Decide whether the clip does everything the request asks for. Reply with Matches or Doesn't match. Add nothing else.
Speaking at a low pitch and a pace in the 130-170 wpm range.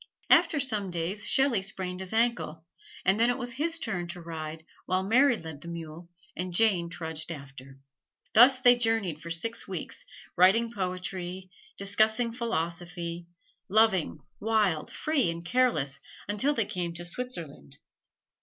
Doesn't match